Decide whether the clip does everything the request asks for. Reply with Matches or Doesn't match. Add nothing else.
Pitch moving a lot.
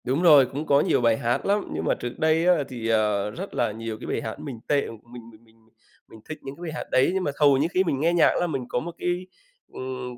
Matches